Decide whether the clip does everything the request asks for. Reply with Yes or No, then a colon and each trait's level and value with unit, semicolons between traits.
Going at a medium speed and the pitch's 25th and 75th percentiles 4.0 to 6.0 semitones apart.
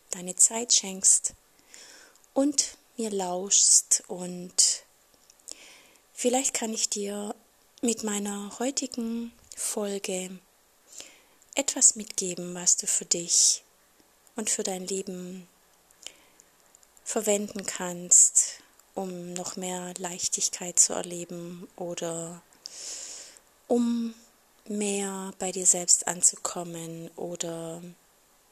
No: slow, 85 wpm; average, 4.4 semitones